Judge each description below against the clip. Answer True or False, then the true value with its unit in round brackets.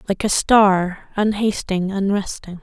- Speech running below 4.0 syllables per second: True (3.8 syllables/s)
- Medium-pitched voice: False (195 Hz)